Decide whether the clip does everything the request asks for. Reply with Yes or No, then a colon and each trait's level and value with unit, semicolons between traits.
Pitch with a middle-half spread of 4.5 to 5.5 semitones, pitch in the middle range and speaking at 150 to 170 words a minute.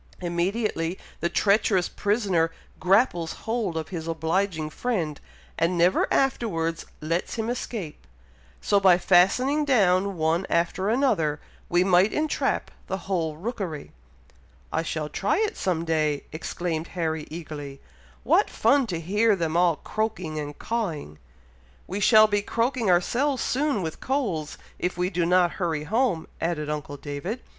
No: average, 4.9 semitones; medium, 180 Hz; average, 140 wpm